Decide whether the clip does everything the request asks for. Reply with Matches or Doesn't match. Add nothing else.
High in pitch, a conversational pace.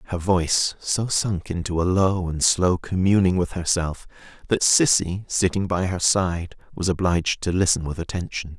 Doesn't match